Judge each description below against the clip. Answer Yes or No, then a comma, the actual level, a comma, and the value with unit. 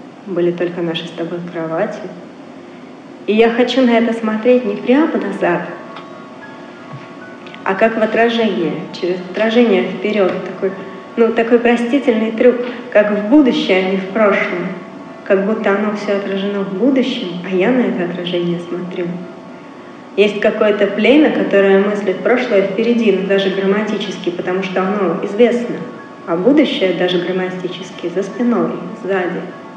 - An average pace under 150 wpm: Yes, average, 135 wpm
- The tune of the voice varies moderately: Yes, average, 3.8 semitones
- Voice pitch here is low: No, high, 200 Hz